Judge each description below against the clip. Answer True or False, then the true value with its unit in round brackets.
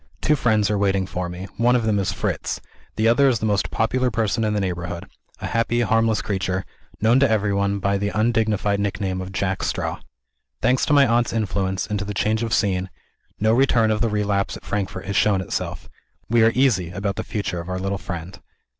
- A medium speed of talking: False (210 wpm)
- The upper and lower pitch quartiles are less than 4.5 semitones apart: True (2.9 semitones)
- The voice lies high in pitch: False (105 Hz)